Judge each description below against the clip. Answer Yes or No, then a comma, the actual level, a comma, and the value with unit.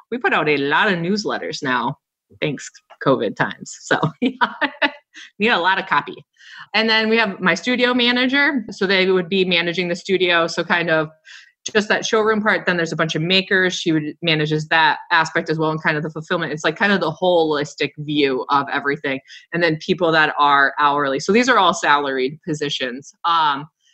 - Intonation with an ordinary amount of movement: Yes, average, 4.7 semitones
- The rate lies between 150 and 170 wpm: No, average, 200 wpm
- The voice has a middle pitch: Yes, medium, 170 Hz